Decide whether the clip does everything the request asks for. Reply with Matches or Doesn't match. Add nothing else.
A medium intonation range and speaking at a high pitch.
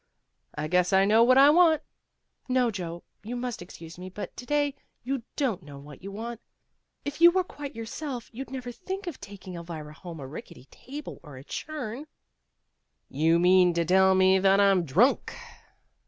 Doesn't match